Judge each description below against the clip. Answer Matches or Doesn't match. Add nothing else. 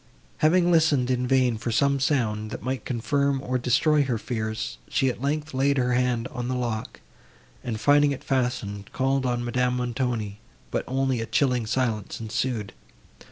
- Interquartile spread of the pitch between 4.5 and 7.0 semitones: Doesn't match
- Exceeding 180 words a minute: Doesn't match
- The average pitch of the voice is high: Doesn't match